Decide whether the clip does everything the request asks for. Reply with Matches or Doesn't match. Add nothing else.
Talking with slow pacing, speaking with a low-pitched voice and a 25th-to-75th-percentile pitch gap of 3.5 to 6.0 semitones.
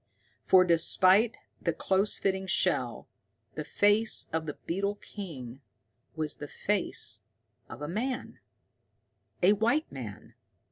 Doesn't match